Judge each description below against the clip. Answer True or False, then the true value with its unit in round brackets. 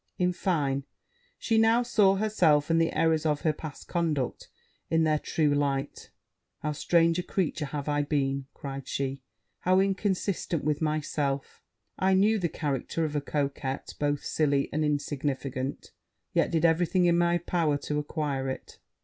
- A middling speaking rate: True (160 wpm)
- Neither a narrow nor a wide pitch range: True (3.3 semitones)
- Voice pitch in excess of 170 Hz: False (155 Hz)